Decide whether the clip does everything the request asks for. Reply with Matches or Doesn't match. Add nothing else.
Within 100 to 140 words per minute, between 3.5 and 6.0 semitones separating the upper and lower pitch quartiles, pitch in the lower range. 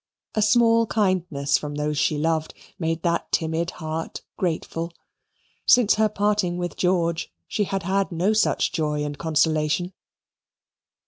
Doesn't match